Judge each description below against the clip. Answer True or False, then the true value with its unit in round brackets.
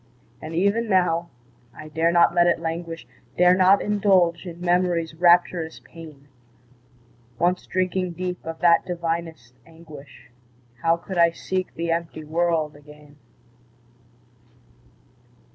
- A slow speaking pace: True (120 wpm)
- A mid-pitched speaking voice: True (170 Hz)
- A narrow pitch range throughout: True (1.7 semitones)